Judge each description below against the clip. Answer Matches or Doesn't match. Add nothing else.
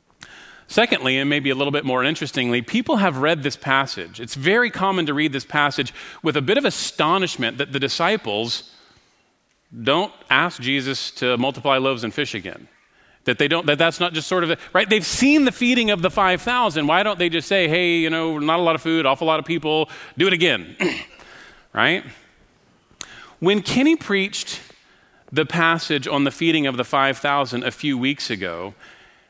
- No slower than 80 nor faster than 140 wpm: Doesn't match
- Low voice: Doesn't match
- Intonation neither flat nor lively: Matches